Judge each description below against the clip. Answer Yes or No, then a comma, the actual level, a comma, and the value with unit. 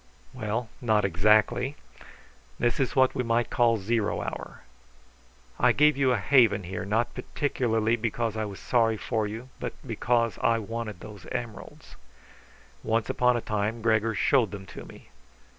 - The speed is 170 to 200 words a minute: No, average, 155 wpm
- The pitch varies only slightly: Yes, narrow, 2.2 semitones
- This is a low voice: Yes, low, 115 Hz